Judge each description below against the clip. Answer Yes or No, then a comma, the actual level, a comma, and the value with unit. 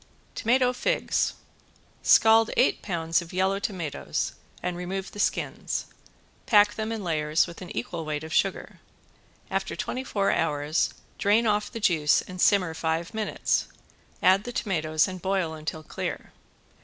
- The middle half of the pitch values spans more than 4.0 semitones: Yes, average, 4.5 semitones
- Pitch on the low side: No, medium, 185 Hz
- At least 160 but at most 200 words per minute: No, average, 145 wpm